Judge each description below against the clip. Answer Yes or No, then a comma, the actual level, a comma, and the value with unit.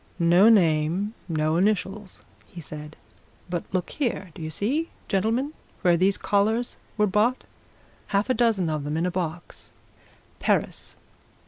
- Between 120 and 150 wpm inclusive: Yes, average, 140 wpm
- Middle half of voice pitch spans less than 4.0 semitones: No, average, 4.4 semitones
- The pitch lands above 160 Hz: Yes, high, 190 Hz